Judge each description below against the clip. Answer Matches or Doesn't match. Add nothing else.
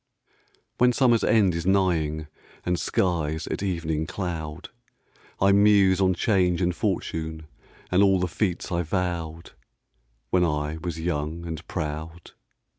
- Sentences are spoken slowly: Matches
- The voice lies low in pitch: Matches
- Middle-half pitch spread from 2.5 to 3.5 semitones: Matches